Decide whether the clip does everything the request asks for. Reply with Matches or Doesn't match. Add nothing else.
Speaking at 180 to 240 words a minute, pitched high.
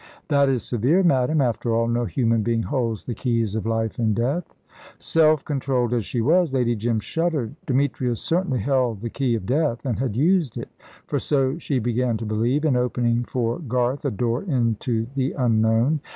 Doesn't match